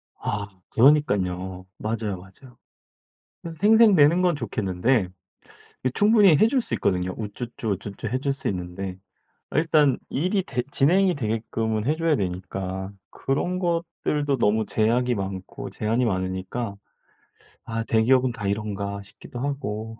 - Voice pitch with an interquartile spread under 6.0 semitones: No, wide, 6.5 semitones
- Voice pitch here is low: Yes, low, 115 Hz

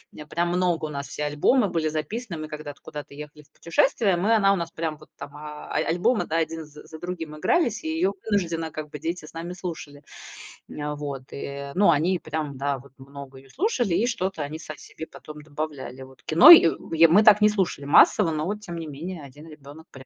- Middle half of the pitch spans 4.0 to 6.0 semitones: No, average, 3.5 semitones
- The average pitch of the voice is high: No, medium, 155 Hz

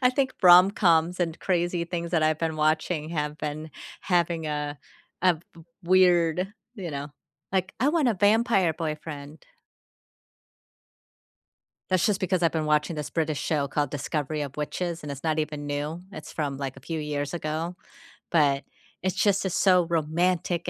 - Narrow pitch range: No, average, 3.1 semitones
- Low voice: No, medium, 165 Hz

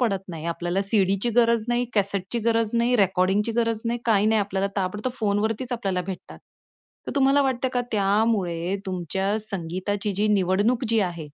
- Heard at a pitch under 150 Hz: No, high, 205 Hz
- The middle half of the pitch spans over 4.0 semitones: No, average, 3.3 semitones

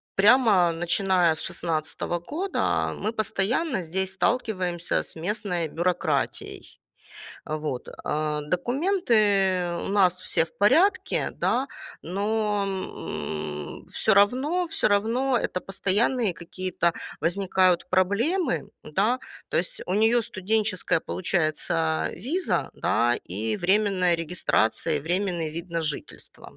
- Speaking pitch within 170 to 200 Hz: Yes, high, 190 Hz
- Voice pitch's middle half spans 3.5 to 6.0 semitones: Yes, average, 4.5 semitones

